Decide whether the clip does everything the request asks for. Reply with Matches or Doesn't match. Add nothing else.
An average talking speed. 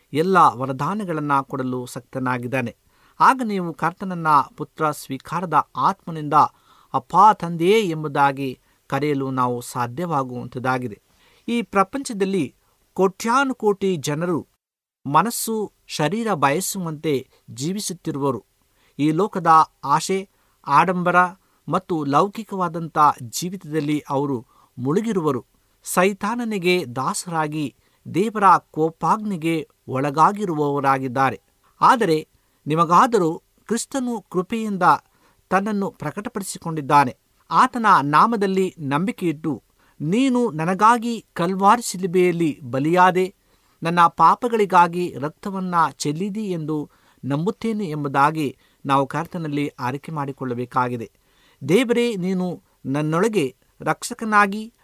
Matches